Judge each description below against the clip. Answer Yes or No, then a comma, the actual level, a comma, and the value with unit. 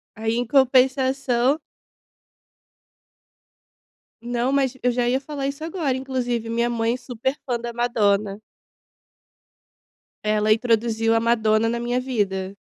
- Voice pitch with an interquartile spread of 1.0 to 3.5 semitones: Yes, narrow, 2.6 semitones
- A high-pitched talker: Yes, high, 240 Hz